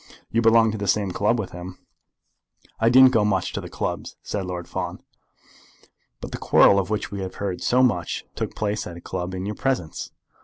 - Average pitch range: Yes, average, 3.5 semitones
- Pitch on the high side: No, low, 100 Hz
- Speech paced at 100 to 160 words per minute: No, fast, 205 wpm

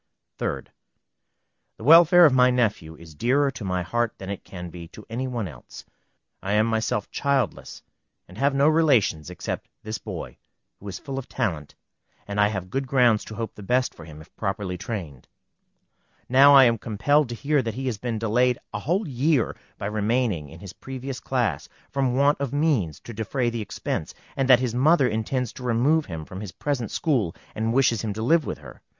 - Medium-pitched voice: No, low, 115 Hz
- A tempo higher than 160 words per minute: Yes, average, 200 wpm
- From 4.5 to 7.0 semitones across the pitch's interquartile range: Yes, average, 5.1 semitones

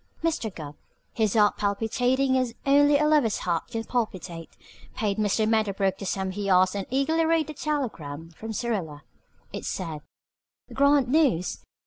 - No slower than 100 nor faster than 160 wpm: Yes, average, 150 wpm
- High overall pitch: Yes, high, 220 Hz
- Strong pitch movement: Yes, wide, 6.5 semitones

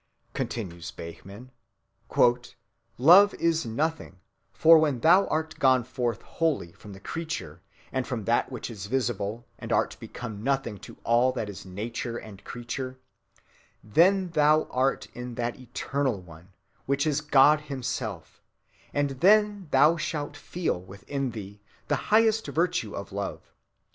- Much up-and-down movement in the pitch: Yes, wide, 6.4 semitones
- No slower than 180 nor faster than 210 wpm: No, average, 140 wpm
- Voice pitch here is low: Yes, low, 130 Hz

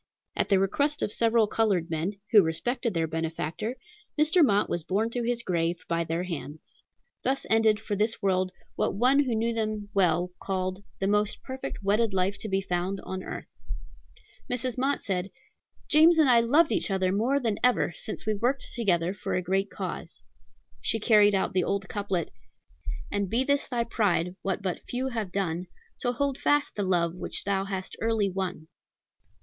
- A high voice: Yes, high, 205 Hz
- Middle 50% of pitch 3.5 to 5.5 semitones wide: Yes, average, 4.1 semitones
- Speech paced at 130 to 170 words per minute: No, average, 180 wpm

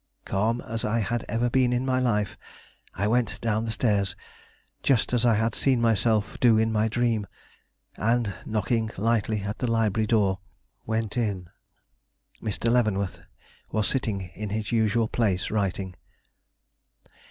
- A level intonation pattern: Yes, narrow, 2.2 semitones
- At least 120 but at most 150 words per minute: Yes, average, 145 wpm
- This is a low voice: Yes, low, 110 Hz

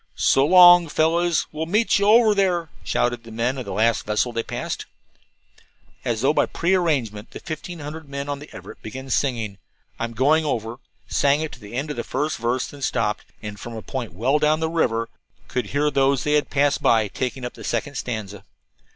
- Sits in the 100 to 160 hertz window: Yes, low, 135 Hz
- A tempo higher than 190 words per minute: Yes, average, 200 wpm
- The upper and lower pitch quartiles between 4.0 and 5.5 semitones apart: Yes, average, 5.1 semitones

